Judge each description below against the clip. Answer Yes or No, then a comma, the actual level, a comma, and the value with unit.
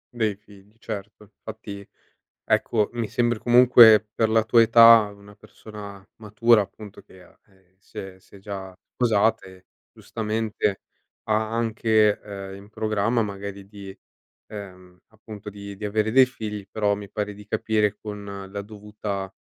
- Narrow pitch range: Yes, narrow, 1.7 semitones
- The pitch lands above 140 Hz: No, low, 105 Hz